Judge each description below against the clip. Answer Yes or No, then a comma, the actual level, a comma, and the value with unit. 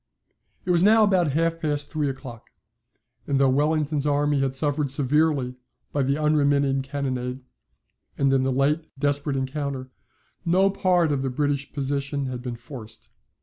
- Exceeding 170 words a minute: No, average, 150 wpm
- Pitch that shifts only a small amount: Yes, narrow, 2.3 semitones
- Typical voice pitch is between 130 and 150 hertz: Yes, medium, 140 Hz